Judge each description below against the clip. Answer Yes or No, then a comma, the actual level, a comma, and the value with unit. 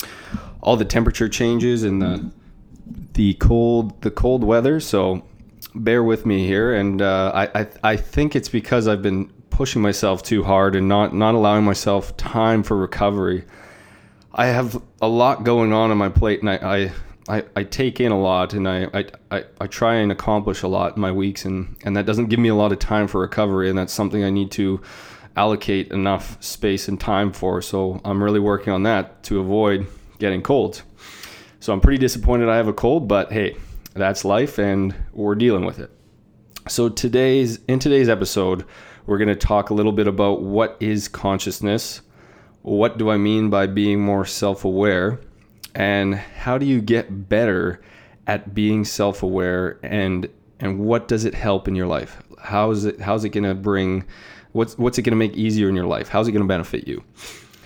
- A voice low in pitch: Yes, low, 105 Hz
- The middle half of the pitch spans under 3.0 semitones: Yes, narrow, 2.4 semitones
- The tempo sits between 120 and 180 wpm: No, average, 190 wpm